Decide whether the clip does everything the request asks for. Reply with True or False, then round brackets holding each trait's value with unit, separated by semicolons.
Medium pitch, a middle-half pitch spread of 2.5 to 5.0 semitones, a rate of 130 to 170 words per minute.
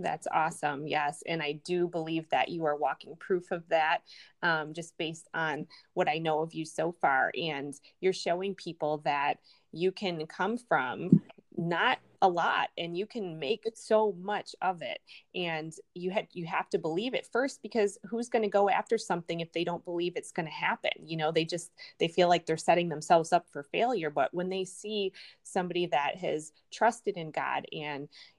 False (175 Hz; 3.1 semitones; 195 wpm)